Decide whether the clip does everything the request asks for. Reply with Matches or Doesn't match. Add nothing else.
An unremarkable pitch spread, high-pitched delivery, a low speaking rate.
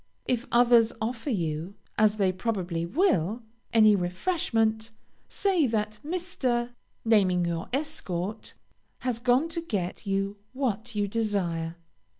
Matches